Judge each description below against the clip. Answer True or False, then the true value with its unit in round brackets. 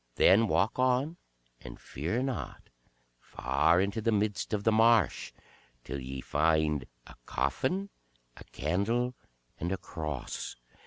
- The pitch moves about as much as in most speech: False (7.4 semitones)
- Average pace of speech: False (125 wpm)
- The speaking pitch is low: True (100 Hz)